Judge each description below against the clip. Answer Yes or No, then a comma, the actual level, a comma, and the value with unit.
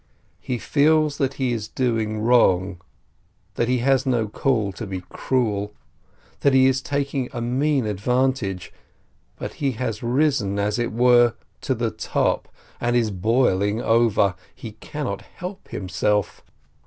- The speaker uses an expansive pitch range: No, average, 4.0 semitones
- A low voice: Yes, low, 120 Hz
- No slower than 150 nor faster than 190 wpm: No, average, 140 wpm